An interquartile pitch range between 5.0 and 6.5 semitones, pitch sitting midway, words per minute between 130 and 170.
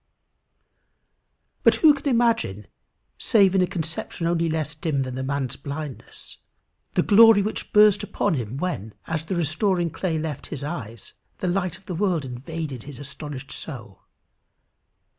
Yes: average, 5.3 semitones; medium, 160 Hz; average, 150 wpm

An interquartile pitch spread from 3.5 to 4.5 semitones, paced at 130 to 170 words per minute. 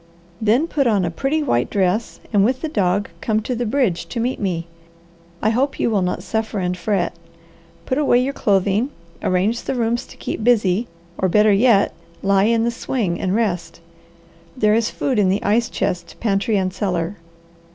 No: average, 4.0 semitones; average, 185 wpm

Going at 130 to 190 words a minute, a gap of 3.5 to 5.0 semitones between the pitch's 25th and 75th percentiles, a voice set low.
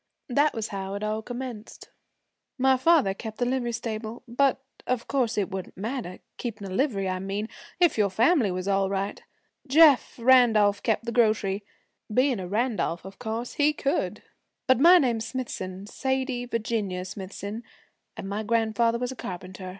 No: average, 165 wpm; average, 4.2 semitones; high, 225 Hz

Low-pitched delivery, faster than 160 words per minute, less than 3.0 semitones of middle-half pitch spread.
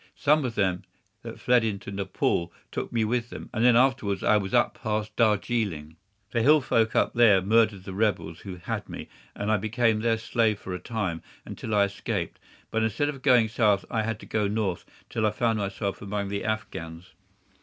Yes: low, 110 Hz; average, 195 wpm; narrow, 2.6 semitones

